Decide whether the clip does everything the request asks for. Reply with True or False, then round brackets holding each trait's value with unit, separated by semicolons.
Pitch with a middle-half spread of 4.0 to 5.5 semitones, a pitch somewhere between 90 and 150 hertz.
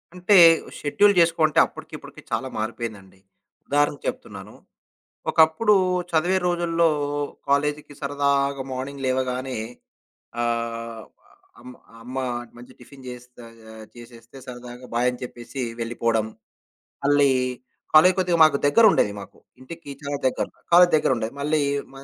True (4.6 semitones; 135 Hz)